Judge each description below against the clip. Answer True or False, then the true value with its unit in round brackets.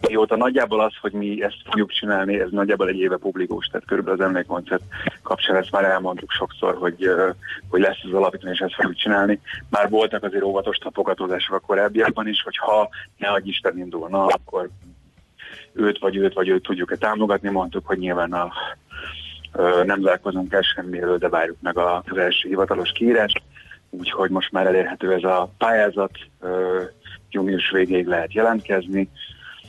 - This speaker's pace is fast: True (165 wpm)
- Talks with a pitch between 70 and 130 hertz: True (95 Hz)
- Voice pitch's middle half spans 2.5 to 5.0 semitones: False (2.0 semitones)